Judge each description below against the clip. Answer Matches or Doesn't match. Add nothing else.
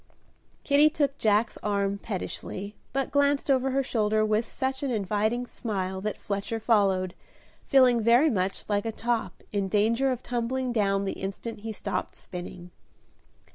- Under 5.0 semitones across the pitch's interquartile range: Matches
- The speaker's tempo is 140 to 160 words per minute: Matches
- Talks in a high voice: Matches